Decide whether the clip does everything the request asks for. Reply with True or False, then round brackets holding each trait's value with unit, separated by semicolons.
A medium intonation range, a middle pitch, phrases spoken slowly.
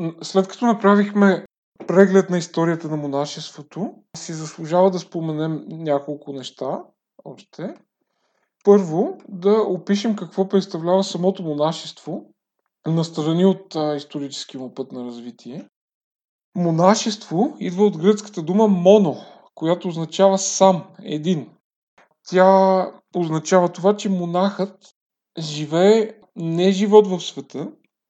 True (3.6 semitones; 180 Hz; 105 wpm)